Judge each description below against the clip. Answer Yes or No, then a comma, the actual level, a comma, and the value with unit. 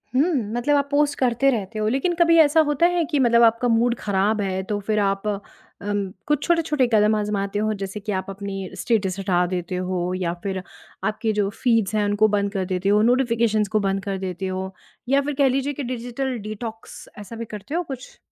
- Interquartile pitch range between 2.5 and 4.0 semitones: No, average, 4.5 semitones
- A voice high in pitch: Yes, high, 215 Hz